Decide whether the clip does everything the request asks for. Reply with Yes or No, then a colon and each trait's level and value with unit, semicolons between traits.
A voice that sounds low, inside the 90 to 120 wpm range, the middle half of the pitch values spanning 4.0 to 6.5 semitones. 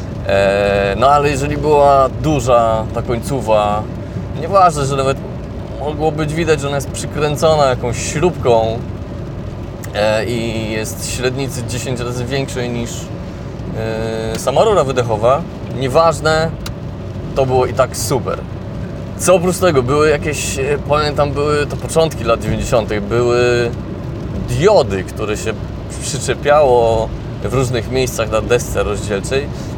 Yes: low, 120 Hz; average, 115 wpm; average, 4.5 semitones